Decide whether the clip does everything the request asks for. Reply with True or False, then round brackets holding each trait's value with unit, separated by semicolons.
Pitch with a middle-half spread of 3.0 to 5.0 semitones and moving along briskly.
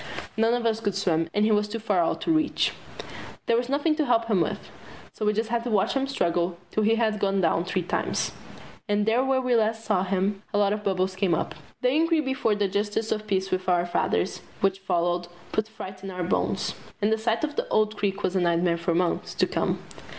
True (3.4 semitones; 235 wpm)